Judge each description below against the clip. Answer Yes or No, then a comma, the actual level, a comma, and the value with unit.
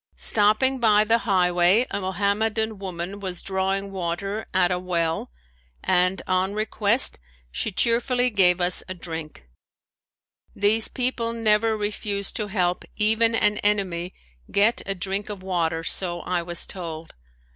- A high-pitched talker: Yes, high, 195 Hz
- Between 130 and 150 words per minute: Yes, slow, 135 wpm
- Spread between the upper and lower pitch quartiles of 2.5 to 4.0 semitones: Yes, average, 3.2 semitones